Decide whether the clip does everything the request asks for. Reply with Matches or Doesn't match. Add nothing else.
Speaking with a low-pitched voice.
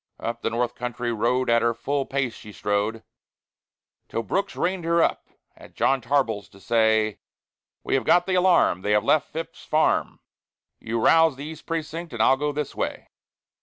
Matches